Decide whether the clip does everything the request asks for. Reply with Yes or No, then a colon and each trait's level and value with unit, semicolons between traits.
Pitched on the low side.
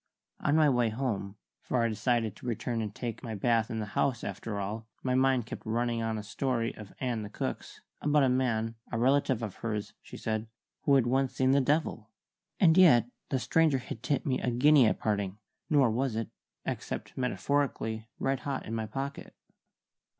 Yes: low, 120 Hz